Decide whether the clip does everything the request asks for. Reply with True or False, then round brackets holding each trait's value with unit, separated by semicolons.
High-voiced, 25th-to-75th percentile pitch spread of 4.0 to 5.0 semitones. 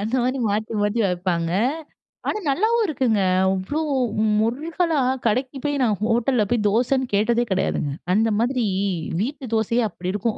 True (235 Hz; 4.5 semitones)